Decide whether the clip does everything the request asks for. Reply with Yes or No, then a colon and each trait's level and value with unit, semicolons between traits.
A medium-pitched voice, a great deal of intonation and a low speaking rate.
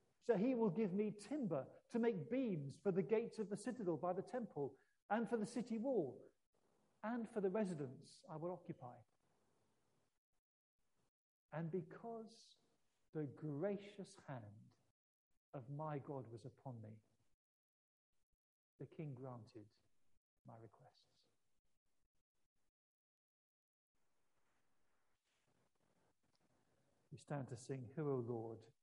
Yes: medium, 160 Hz; wide, 8.4 semitones; slow, 110 wpm